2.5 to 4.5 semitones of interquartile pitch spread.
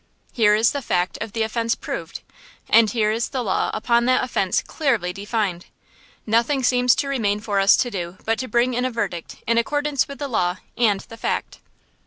Yes: average, 3.3 semitones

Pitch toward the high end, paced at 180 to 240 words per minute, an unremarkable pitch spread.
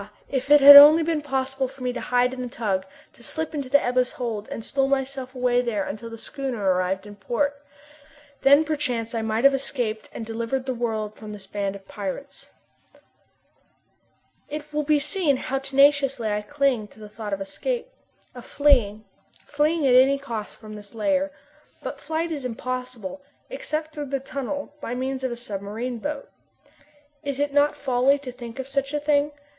Yes: very high, 260 Hz; average, 185 wpm; average, 4.0 semitones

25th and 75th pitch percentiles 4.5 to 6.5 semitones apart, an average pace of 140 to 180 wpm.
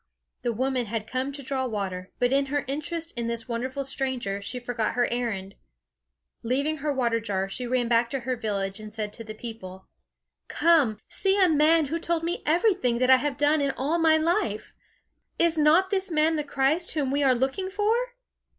No: average, 5.2 semitones; average, 195 wpm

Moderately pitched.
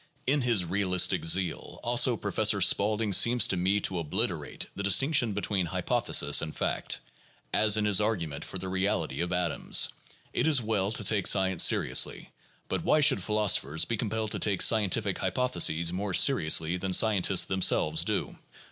No: low, 100 Hz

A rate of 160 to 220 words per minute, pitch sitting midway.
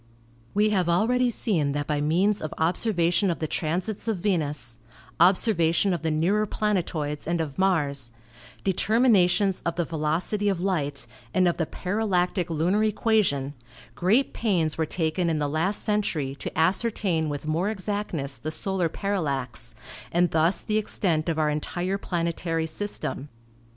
No: average, 150 wpm; medium, 175 Hz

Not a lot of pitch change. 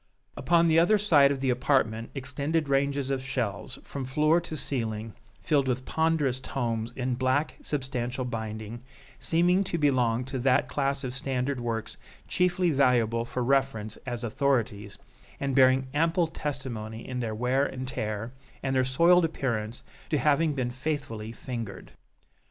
No: average, 3.4 semitones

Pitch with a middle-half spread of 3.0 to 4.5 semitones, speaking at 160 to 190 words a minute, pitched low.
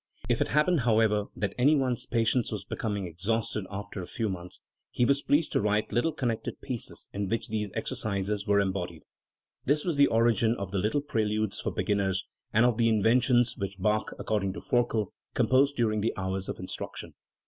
Yes: average, 3.3 semitones; average, 185 wpm; low, 110 Hz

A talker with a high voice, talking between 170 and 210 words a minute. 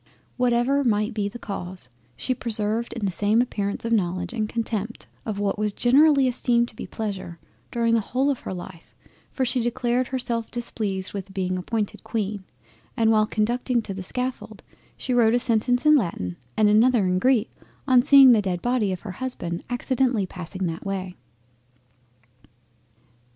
No: high, 220 Hz; average, 160 wpm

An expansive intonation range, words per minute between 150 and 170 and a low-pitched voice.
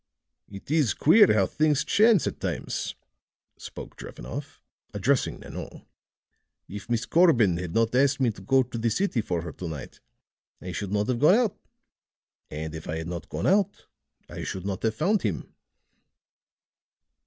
Yes: wide, 8.7 semitones; average, 165 wpm; low, 115 Hz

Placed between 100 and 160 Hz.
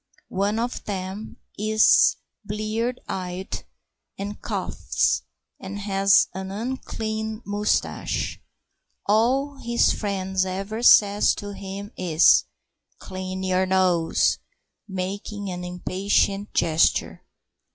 No: high, 200 Hz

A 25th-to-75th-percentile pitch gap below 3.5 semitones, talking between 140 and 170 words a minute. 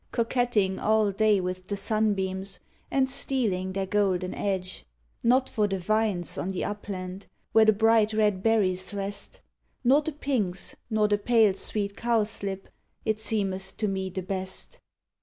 Yes: narrow, 2.6 semitones; average, 150 wpm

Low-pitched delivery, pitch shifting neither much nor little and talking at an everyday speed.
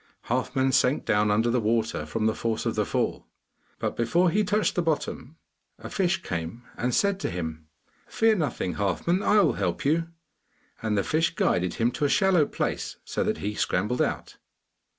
No: low, 125 Hz; wide, 8.0 semitones; average, 185 wpm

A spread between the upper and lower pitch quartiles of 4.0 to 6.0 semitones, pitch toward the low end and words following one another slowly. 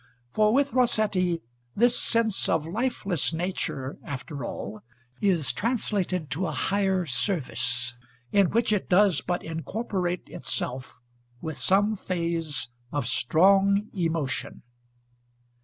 No: average, 4.8 semitones; medium, 180 Hz; slow, 110 wpm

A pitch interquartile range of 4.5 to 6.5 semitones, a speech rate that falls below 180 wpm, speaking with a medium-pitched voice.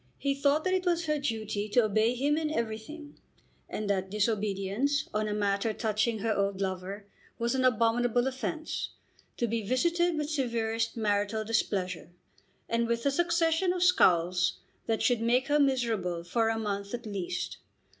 No: average, 5.3 semitones; average, 165 wpm; high, 230 Hz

